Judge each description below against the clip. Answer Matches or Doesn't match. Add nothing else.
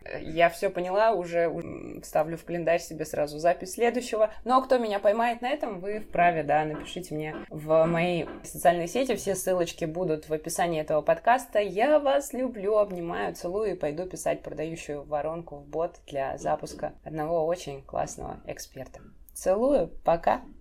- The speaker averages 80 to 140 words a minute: Doesn't match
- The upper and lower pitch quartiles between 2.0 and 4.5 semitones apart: Doesn't match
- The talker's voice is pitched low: Doesn't match